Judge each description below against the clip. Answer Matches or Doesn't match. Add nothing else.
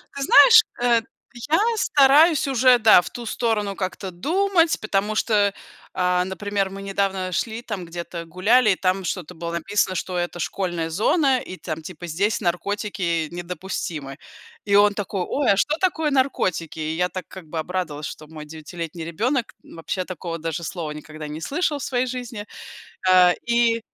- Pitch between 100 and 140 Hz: Doesn't match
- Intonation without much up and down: Doesn't match